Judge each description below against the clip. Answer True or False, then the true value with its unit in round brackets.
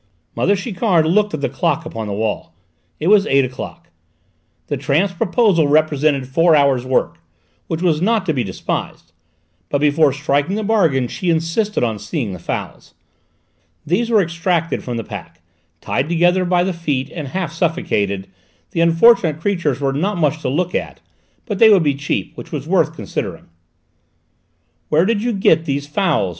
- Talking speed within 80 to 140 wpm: False (170 wpm)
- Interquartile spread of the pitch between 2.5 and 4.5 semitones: False (5.0 semitones)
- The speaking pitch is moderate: True (160 Hz)